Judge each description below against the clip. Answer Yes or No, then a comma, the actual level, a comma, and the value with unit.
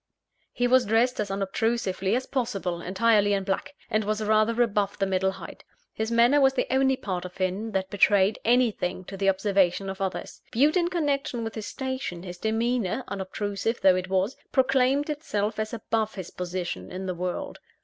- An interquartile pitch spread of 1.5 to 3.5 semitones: No, average, 4.2 semitones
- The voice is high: Yes, high, 210 Hz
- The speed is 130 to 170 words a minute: No, average, 180 wpm